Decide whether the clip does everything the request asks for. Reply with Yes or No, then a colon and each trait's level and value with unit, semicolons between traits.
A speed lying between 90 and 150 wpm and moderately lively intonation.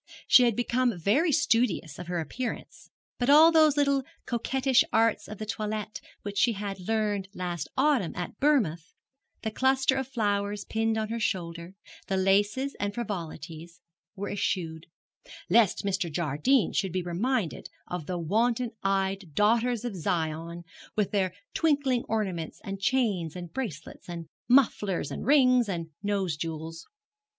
No: average, 145 wpm; wide, 5.7 semitones